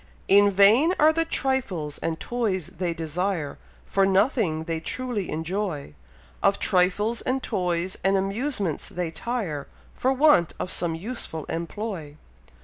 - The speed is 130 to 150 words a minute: Yes, slow, 135 wpm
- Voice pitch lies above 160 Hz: Yes, high, 190 Hz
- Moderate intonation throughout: No, wide, 5.9 semitones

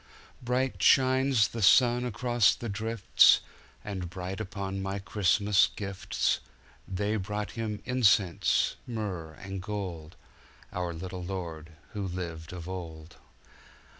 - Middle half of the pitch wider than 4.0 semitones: No, average, 3.4 semitones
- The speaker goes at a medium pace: No, slow, 105 wpm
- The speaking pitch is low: Yes, very low, 95 Hz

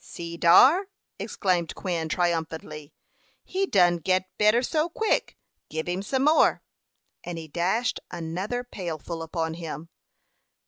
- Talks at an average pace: No, slow, 125 wpm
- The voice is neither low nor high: Yes, medium, 175 Hz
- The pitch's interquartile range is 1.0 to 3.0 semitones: No, average, 4.8 semitones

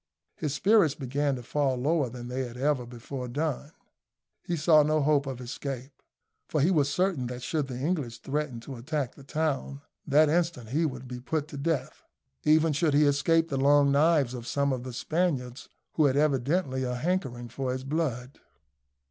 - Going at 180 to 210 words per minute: Yes, average, 185 wpm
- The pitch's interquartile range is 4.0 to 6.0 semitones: No, average, 3.2 semitones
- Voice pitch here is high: No, medium, 140 Hz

